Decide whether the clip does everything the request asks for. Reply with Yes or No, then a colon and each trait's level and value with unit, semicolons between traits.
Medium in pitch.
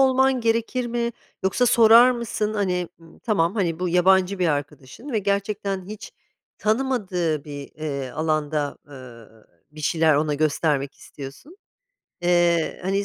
Yes: medium, 180 Hz